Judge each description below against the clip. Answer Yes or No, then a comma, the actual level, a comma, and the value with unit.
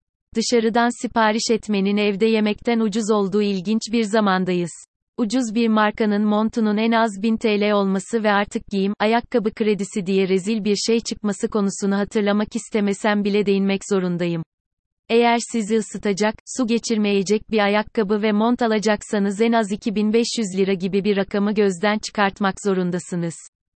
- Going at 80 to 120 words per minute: No, fast, 140 wpm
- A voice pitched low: No, high, 210 Hz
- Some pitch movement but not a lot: No, narrow, 2.2 semitones